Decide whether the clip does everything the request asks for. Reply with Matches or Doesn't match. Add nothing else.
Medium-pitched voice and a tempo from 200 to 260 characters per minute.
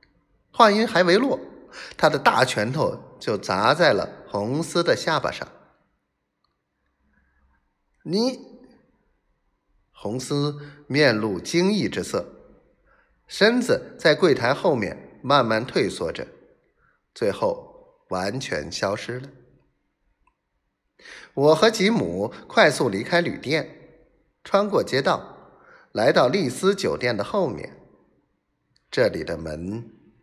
Doesn't match